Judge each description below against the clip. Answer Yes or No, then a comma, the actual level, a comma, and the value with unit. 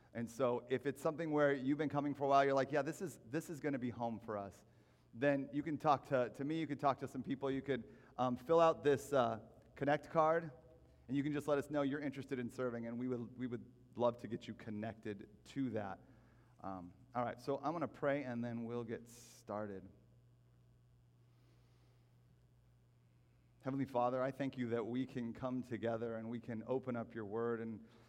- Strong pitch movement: No, average, 3.0 semitones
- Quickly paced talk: Yes, fast, 215 wpm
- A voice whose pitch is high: No, low, 125 Hz